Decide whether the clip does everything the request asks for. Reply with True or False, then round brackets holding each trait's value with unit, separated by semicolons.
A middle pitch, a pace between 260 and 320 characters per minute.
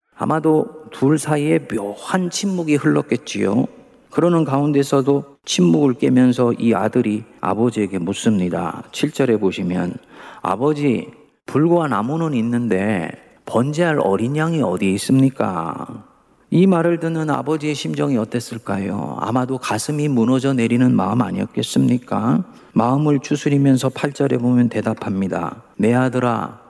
False (130 Hz; 300 characters per minute)